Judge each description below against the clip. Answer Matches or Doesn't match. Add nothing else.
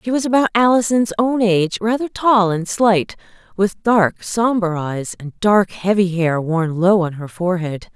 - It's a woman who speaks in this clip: Matches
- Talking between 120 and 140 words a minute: Doesn't match